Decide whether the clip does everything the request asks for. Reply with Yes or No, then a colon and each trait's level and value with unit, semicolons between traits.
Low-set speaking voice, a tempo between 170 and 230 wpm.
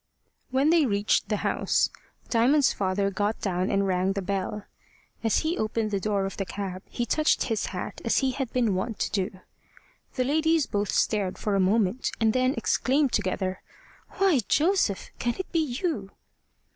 No: high, 215 Hz; average, 175 wpm